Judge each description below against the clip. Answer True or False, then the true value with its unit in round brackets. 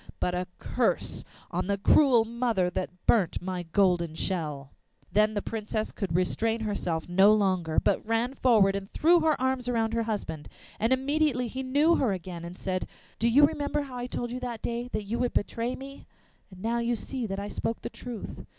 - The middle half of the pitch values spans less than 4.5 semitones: False (4.8 semitones)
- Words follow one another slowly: False (195 wpm)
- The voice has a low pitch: False (225 Hz)